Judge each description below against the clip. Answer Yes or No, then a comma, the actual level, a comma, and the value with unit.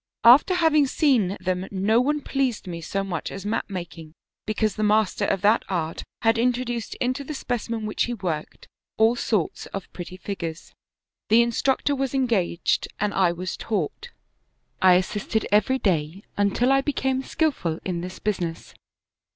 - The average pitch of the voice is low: No, high, 210 Hz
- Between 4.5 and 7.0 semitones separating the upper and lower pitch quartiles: Yes, average, 5.3 semitones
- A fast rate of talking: No, average, 165 wpm